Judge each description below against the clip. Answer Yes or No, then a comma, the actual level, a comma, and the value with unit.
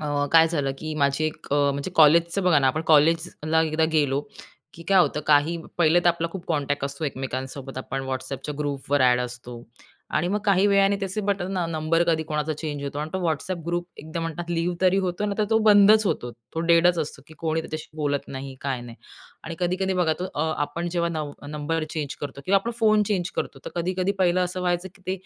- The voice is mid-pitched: Yes, medium, 160 Hz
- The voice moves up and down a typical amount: Yes, average, 3.7 semitones